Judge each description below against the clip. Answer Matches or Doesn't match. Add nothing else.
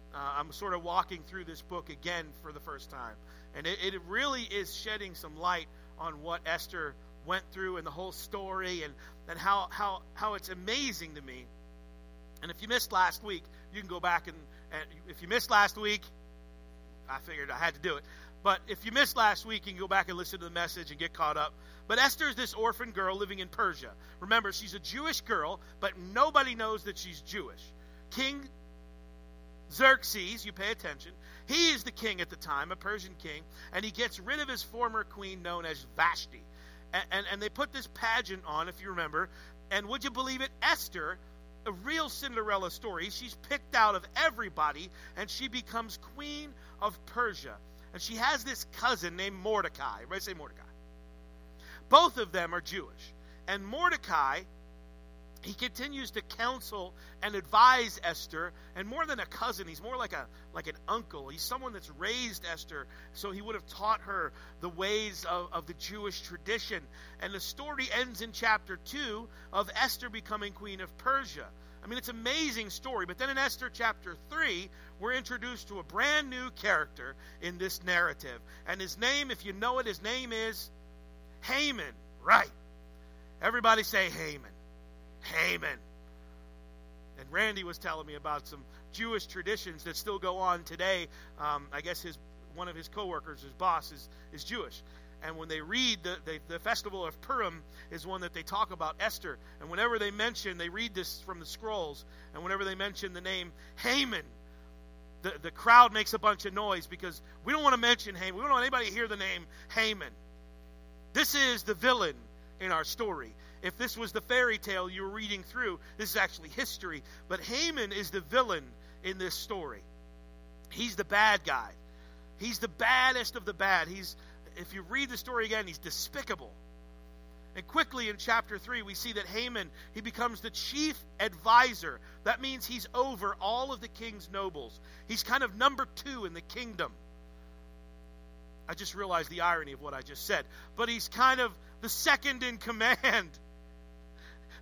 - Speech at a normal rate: Matches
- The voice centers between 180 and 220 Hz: Matches